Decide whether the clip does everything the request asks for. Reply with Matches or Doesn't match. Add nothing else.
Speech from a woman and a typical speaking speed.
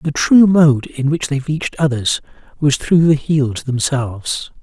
Doesn't match